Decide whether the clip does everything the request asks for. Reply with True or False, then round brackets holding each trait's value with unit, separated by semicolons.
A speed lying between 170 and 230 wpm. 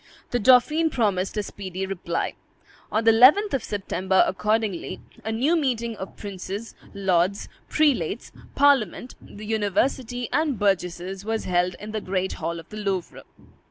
False (145 wpm)